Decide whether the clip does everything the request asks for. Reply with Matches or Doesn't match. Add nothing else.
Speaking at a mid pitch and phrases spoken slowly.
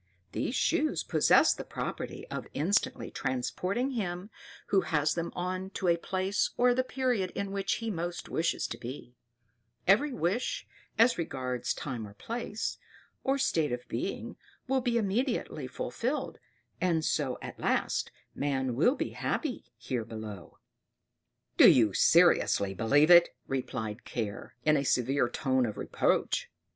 Doesn't match